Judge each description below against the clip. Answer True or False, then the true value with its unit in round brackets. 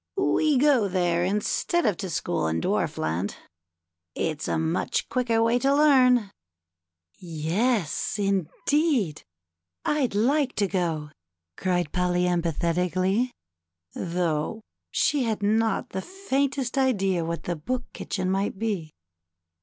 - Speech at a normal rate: False (120 wpm)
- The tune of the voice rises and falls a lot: True (6.7 semitones)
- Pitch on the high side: True (195 Hz)